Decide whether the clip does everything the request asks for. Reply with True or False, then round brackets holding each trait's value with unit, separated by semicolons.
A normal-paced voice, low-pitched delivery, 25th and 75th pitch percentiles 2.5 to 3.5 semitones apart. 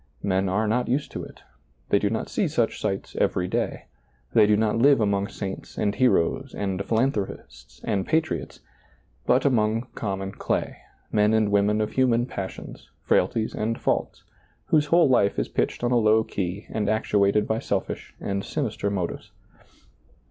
True (165 wpm; 105 Hz; 3.1 semitones)